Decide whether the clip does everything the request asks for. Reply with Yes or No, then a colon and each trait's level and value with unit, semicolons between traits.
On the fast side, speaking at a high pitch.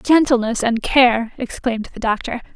No: average, 140 wpm; high, 240 Hz